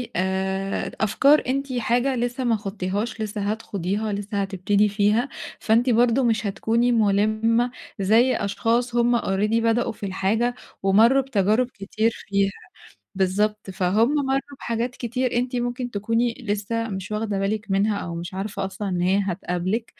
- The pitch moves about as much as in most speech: Yes, average, 3.3 semitones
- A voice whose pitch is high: Yes, high, 215 Hz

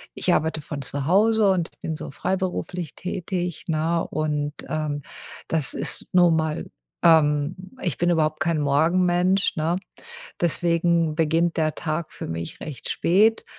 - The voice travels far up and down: No, narrow, 2.4 semitones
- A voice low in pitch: No, medium, 165 Hz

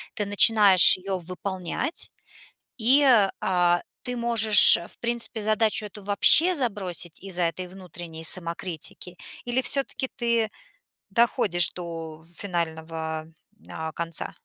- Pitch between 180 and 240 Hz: Yes, high, 190 Hz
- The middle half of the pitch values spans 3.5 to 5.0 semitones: Yes, average, 4.7 semitones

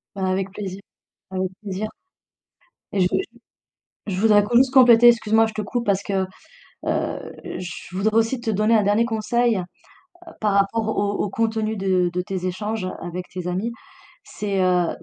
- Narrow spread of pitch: No, average, 3.0 semitones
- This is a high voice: Yes, high, 205 Hz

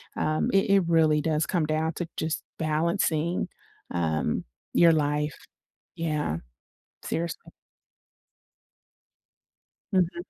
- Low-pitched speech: No, medium, 160 Hz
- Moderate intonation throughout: No, narrow, 2.0 semitones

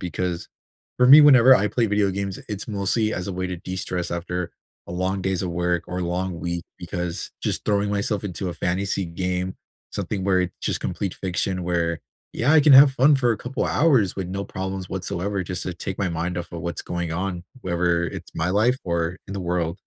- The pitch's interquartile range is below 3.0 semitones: Yes, narrow, 2.4 semitones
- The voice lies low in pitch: Yes, very low, 95 Hz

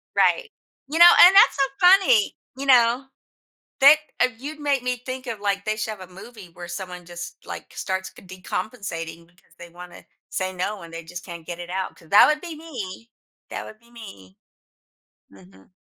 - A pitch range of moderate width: No, wide, 6.5 semitones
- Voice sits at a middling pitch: No, high, 200 Hz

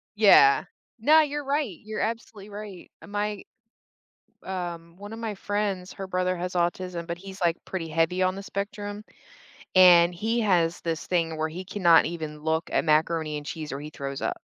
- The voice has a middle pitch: Yes, medium, 180 Hz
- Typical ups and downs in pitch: Yes, average, 3.7 semitones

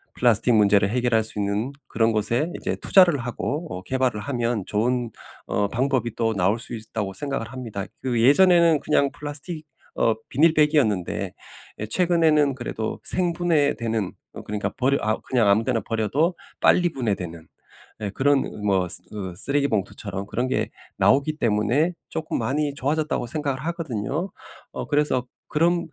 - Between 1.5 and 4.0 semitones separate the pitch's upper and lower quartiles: No, wide, 5.6 semitones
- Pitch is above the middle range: No, low, 125 Hz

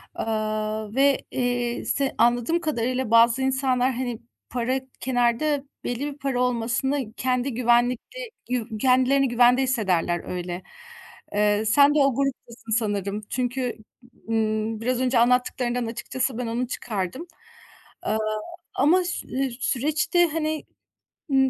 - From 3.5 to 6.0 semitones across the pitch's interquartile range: No, average, 2.8 semitones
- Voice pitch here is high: Yes, high, 245 Hz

